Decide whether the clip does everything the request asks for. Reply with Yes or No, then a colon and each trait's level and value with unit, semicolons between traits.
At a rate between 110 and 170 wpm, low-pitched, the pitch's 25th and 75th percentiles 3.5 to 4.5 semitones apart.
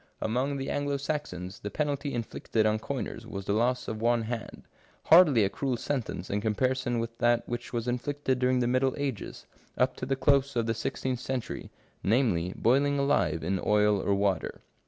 No: average, 180 wpm; low, 120 Hz; average, 3.9 semitones